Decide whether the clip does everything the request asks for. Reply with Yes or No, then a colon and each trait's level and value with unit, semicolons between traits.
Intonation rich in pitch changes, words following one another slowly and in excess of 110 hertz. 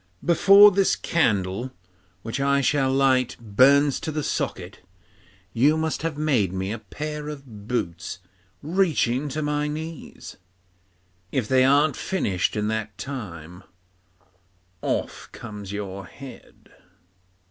Yes: wide, 6.3 semitones; slow, 120 wpm; low, 135 Hz